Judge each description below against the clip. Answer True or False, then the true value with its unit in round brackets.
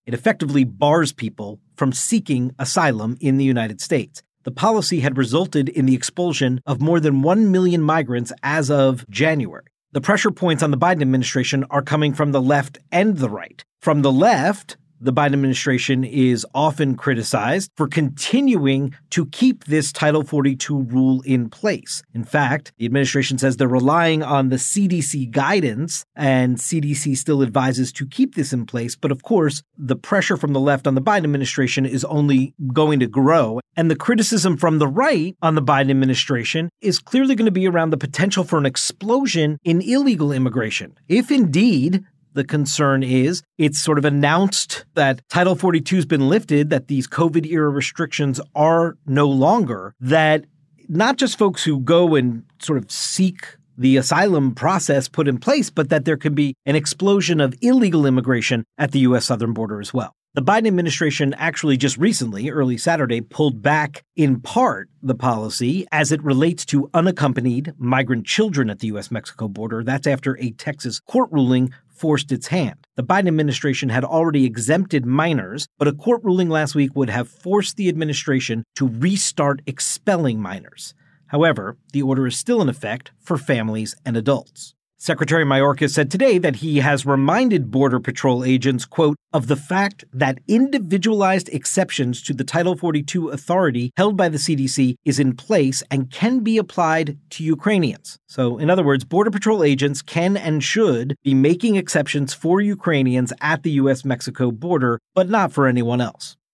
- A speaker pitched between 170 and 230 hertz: False (145 Hz)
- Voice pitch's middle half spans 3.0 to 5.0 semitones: True (4.1 semitones)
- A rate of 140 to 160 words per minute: False (170 wpm)